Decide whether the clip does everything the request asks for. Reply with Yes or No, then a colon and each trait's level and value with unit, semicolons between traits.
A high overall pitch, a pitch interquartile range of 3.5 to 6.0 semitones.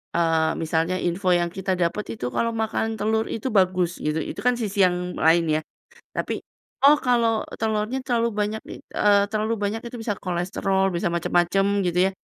Yes: high, 195 Hz; average, 4.1 semitones